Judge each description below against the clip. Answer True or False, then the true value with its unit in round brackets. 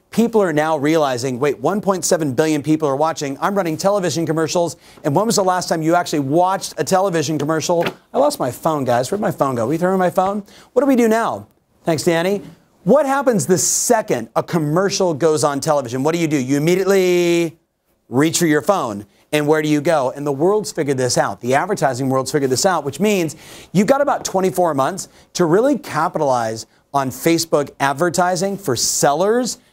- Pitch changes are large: False (4.2 semitones)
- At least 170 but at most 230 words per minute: True (200 wpm)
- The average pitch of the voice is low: False (165 Hz)